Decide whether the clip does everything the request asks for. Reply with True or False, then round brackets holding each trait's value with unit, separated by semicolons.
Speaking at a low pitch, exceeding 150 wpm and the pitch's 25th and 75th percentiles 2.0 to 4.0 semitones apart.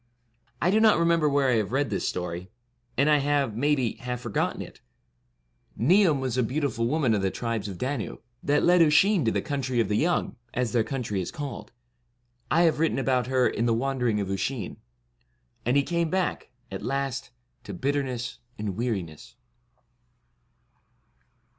False (130 Hz; 170 wpm; 4.6 semitones)